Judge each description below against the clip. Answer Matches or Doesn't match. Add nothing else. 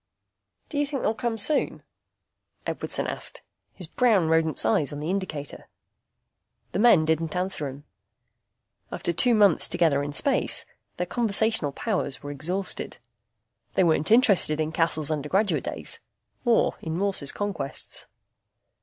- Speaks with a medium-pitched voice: Matches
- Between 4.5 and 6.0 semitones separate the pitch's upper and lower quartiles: Matches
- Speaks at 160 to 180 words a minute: Doesn't match